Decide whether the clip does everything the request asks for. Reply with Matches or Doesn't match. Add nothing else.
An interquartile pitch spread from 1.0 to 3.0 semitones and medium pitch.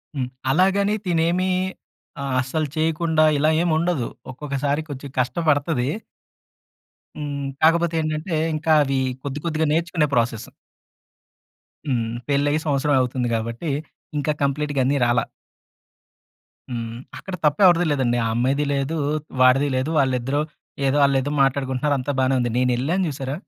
Doesn't match